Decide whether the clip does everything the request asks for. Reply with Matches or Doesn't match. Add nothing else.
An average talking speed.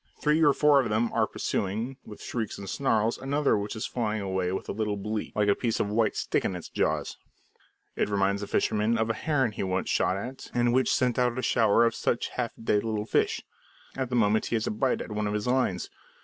Doesn't match